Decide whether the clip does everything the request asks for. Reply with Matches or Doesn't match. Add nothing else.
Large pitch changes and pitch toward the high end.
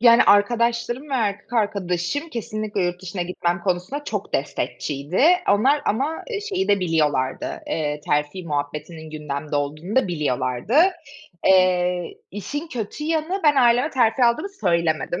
Matches